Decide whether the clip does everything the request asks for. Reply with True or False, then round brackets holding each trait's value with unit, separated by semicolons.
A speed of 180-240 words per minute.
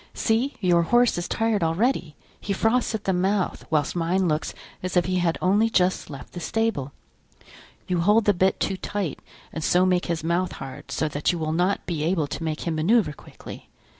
True (200 wpm)